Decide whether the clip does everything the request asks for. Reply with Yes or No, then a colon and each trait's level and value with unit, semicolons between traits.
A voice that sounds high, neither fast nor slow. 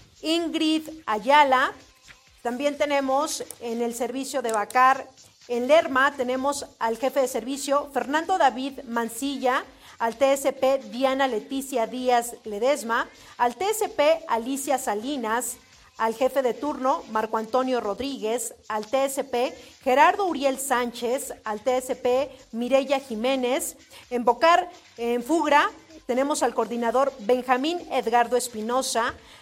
No: very high, 260 Hz; slow, 110 wpm